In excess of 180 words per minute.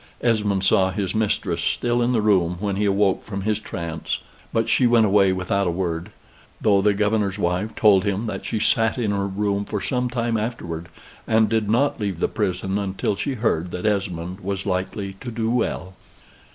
Yes: average, 190 wpm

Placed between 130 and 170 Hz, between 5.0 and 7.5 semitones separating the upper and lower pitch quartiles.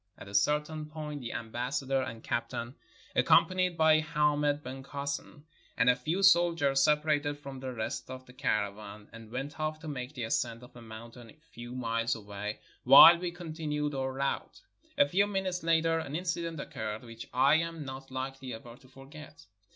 No: medium, 140 Hz; average, 4.3 semitones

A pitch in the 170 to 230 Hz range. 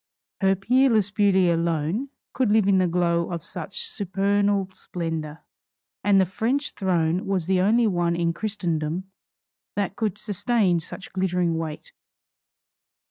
Yes: high, 190 Hz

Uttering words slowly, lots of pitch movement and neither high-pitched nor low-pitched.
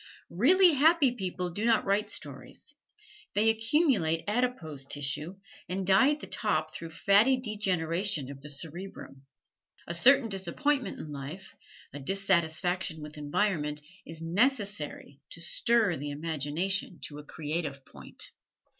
Yes: slow, 130 wpm; wide, 6.0 semitones; medium, 180 Hz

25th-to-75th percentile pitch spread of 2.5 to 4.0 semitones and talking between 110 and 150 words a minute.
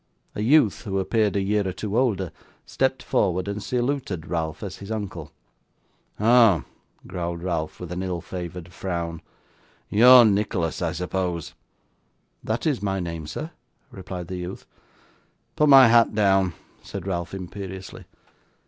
Yes: average, 3.6 semitones; average, 145 wpm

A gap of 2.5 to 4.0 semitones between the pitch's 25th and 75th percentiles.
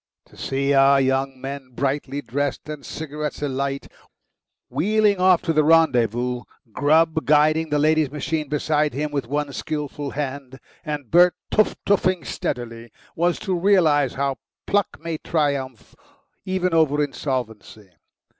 Yes: average, 2.9 semitones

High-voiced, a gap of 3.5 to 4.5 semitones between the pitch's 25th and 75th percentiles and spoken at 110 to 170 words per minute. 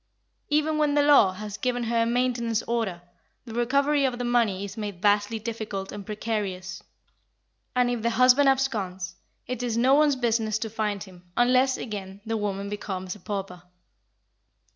Yes: high, 225 Hz; average, 3.8 semitones; average, 165 wpm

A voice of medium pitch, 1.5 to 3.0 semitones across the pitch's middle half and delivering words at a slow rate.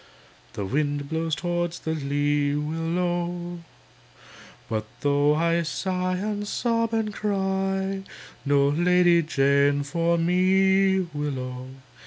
No: medium, 170 Hz; average, 4.6 semitones; slow, 105 wpm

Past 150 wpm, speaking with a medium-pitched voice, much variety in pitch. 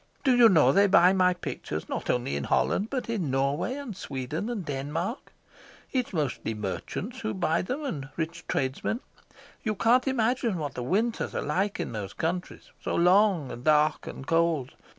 Yes: average, 175 wpm; medium, 175 Hz; wide, 7.6 semitones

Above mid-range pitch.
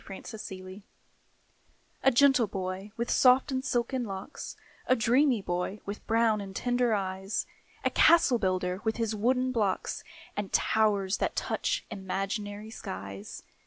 Yes: high, 215 Hz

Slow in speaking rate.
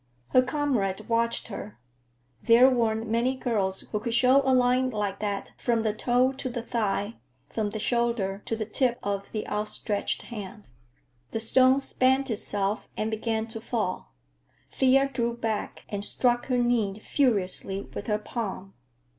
No: average, 155 wpm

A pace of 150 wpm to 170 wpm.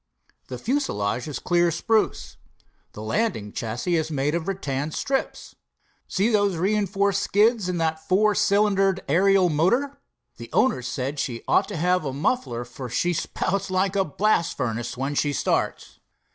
Yes: average, 155 wpm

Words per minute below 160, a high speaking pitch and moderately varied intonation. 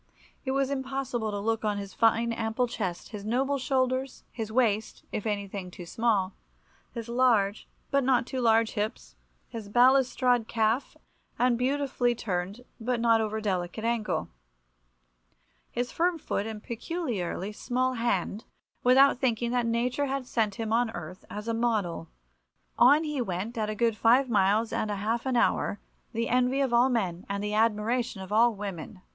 No: average, 165 wpm; high, 230 Hz; average, 3.1 semitones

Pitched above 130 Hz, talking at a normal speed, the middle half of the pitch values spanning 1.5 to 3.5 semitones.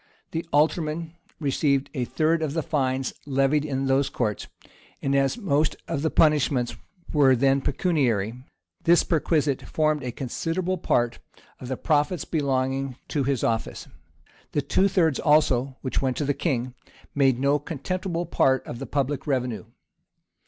Yes: medium, 140 Hz; average, 150 wpm; average, 2.9 semitones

